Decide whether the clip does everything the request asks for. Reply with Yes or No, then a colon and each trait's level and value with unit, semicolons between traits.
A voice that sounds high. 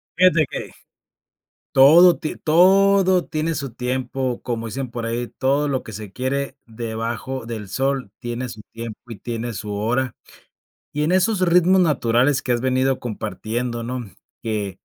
No: low, 130 Hz